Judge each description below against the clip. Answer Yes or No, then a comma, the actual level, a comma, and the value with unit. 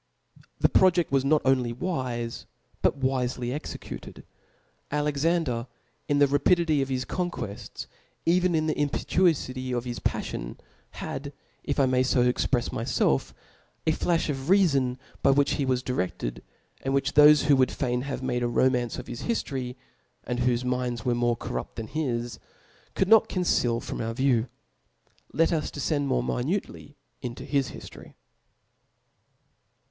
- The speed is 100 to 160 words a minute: Yes, average, 155 wpm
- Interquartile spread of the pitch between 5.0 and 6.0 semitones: No, average, 3.3 semitones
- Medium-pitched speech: No, low, 130 Hz